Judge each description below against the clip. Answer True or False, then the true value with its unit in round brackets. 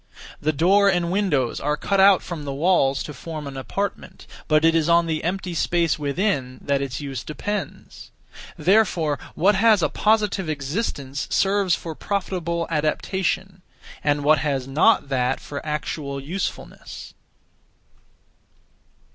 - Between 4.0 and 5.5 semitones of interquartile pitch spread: True (5.0 semitones)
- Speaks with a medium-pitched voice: True (160 Hz)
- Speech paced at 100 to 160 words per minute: True (140 wpm)